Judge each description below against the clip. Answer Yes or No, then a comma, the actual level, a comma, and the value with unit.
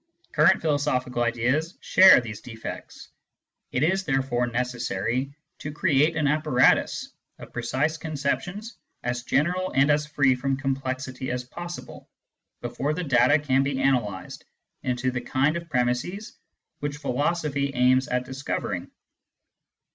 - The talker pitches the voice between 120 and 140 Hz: Yes, low, 135 Hz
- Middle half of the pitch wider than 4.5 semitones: No, average, 3.3 semitones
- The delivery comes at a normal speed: No, slow, 130 wpm